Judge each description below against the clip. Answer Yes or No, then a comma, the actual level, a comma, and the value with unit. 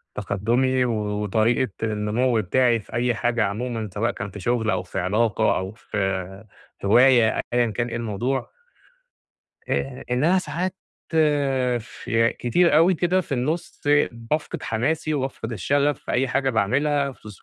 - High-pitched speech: No, low, 120 Hz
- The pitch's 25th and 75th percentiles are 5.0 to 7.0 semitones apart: No, average, 4.0 semitones